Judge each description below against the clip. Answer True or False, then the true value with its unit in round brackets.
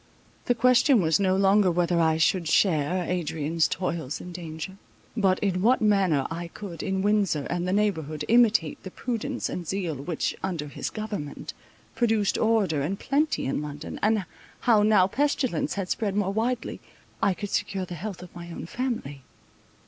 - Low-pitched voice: False (190 Hz)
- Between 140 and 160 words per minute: False (170 wpm)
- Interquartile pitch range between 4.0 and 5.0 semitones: True (4.4 semitones)